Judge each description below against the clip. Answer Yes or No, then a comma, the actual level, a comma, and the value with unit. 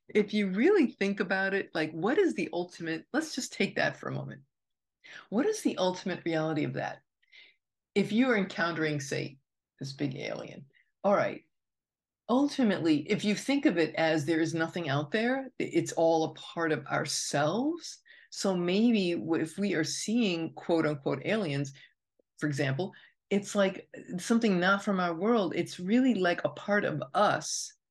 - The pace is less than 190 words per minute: Yes, average, 170 wpm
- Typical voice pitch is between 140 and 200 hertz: Yes, medium, 185 Hz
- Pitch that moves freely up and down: Yes, wide, 5.7 semitones